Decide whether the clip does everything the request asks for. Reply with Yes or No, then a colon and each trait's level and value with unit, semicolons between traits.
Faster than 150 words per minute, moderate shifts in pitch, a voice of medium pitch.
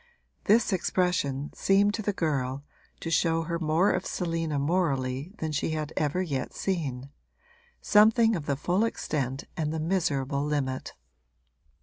No: average, 140 wpm; average, 4.7 semitones; medium, 160 Hz